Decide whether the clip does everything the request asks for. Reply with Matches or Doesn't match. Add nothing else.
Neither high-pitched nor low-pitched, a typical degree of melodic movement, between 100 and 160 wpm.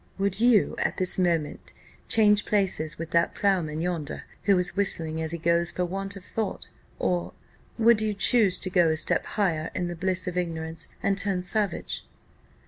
Doesn't match